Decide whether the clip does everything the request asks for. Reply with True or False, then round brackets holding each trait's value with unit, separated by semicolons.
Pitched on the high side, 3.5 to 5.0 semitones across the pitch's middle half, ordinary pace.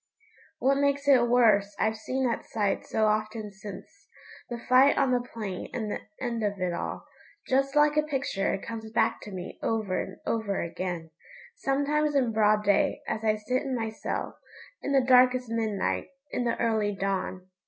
True (225 Hz; 3.8 semitones; 180 wpm)